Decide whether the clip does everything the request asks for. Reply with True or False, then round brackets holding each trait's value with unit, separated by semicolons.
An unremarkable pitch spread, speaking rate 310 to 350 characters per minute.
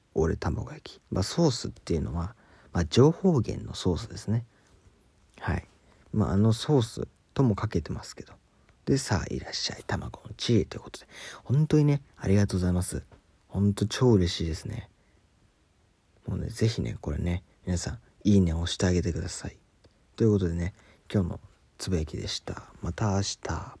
True (3.7 semitones; 340 characters per minute)